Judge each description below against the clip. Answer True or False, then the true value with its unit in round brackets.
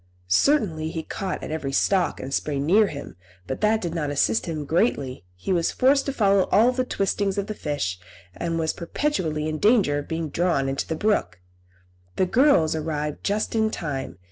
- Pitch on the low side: False (165 Hz)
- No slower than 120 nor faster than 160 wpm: False (190 wpm)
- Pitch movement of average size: False (5.9 semitones)